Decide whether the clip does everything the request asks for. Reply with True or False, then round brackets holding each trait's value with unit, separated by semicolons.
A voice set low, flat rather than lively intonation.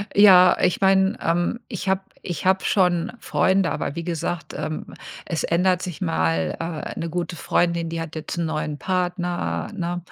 False (175 Hz; 2.3 semitones)